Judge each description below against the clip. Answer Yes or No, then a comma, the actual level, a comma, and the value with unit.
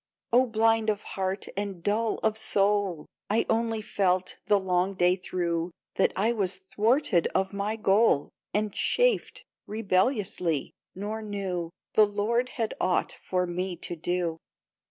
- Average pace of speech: Yes, average, 145 wpm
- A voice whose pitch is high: Yes, high, 200 Hz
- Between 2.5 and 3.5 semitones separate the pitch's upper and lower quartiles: Yes, average, 3.2 semitones